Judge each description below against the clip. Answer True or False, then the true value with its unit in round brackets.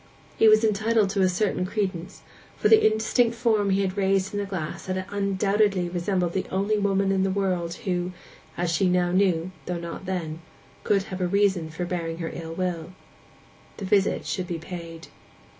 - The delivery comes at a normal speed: True (175 wpm)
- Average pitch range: False (2.3 semitones)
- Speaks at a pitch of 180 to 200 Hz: True (190 Hz)